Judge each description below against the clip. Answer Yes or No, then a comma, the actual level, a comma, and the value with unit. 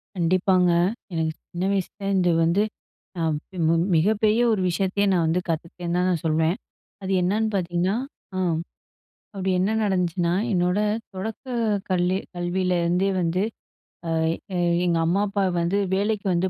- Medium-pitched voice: Yes, medium, 180 Hz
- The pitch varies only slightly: Yes, narrow, 2.3 semitones